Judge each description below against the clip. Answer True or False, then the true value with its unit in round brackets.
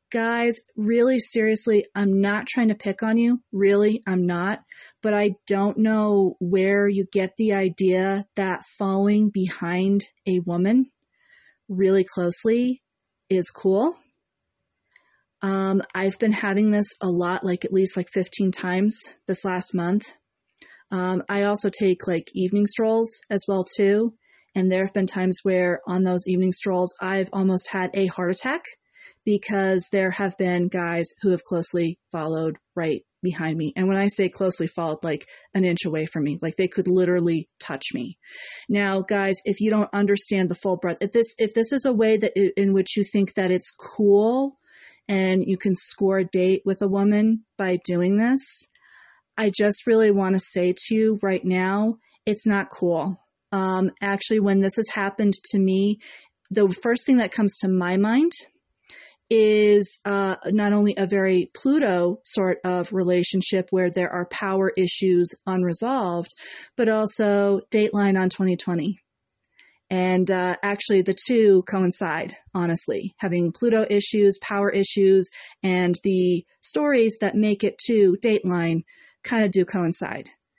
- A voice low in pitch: False (195 Hz)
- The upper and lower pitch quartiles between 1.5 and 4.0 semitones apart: True (2.4 semitones)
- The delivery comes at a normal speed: True (160 wpm)